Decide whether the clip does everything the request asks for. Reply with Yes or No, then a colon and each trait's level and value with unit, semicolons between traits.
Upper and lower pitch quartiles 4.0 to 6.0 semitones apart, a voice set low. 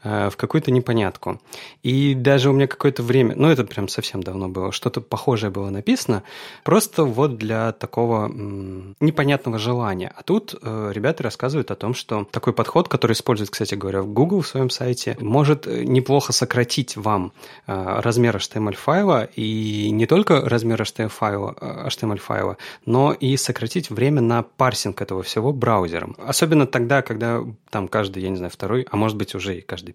Yes: average, 4.4 semitones; low, 115 Hz